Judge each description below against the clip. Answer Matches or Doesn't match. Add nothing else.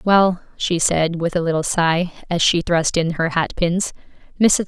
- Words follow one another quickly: Doesn't match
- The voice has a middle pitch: Matches